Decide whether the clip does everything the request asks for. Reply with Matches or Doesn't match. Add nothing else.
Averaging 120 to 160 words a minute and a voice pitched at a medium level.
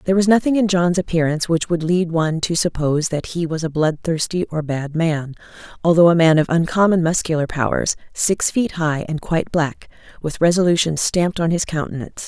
Doesn't match